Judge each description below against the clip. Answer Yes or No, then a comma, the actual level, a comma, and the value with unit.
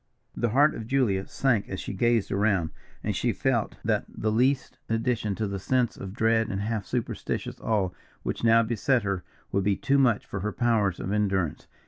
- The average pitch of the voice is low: Yes, low, 110 Hz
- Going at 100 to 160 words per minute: No, average, 190 wpm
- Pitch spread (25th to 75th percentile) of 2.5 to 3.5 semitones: Yes, average, 3.2 semitones